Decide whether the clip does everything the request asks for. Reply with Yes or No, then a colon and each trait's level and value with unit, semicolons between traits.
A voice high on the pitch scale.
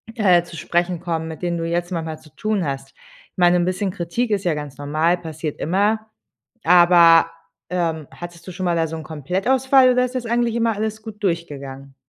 No: medium, 175 Hz